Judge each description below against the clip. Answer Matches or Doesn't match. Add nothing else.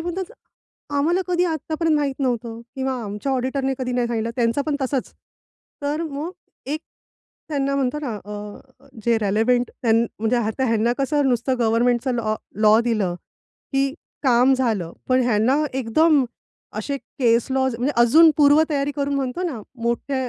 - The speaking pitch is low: Doesn't match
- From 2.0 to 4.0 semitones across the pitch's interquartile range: Matches